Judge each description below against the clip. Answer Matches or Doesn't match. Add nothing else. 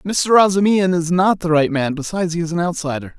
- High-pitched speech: Doesn't match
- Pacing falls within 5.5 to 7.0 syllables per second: Matches